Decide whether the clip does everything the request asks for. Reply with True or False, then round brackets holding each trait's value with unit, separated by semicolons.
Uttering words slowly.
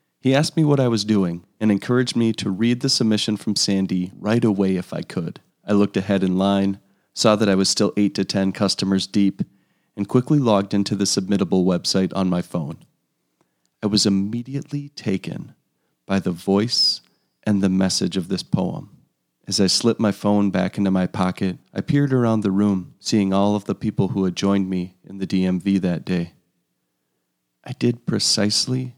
False (185 wpm)